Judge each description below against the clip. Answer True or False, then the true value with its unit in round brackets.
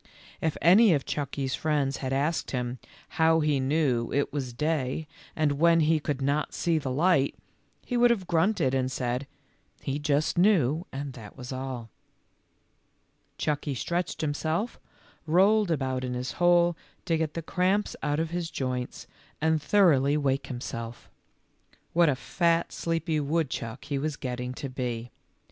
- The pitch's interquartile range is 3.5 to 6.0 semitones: True (4.0 semitones)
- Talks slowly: False (155 wpm)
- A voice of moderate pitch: True (145 Hz)